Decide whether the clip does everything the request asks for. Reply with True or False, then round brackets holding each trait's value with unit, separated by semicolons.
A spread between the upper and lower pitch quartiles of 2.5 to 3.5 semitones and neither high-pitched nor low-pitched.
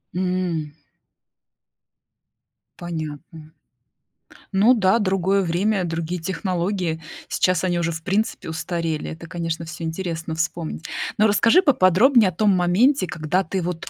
True (2.9 semitones; 180 Hz)